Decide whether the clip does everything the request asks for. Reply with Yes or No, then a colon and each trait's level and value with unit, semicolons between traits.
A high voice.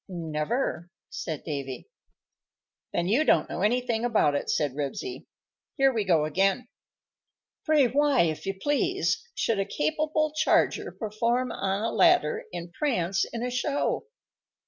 Yes: high, 225 Hz